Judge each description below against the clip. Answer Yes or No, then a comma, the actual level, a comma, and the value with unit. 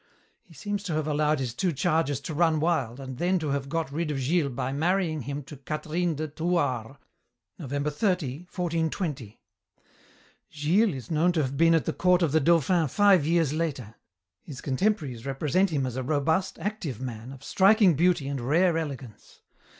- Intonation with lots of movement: No, average, 4.1 semitones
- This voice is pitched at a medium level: Yes, medium, 155 Hz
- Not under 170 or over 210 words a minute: Yes, average, 180 wpm